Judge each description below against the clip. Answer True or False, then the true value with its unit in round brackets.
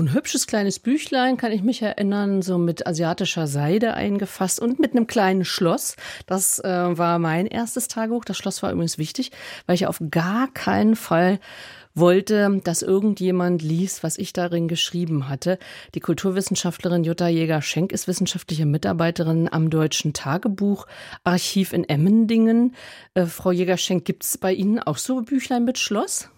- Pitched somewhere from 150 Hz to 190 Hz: True (185 Hz)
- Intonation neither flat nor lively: True (4.6 semitones)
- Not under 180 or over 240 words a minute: False (155 wpm)